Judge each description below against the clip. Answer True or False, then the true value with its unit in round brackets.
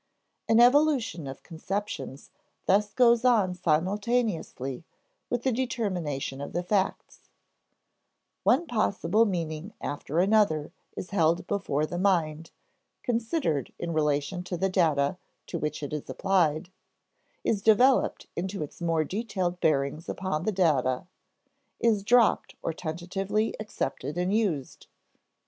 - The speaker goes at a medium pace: False (120 wpm)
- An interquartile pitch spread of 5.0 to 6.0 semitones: True (5.4 semitones)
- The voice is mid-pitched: True (180 Hz)